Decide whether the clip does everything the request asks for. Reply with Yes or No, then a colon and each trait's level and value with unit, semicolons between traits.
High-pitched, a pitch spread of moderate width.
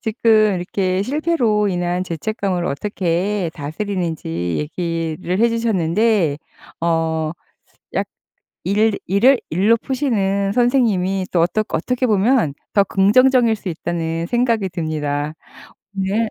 Yes: high, 195 Hz; average, 4.8 semitones